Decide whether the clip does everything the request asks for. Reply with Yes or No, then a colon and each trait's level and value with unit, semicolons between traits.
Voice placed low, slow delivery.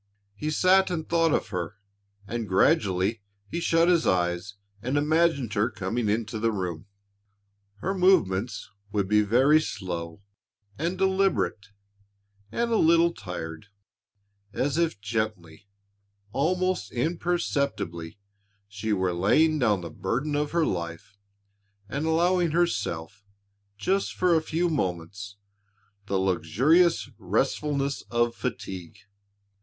Yes: low, 120 Hz; slow, 115 wpm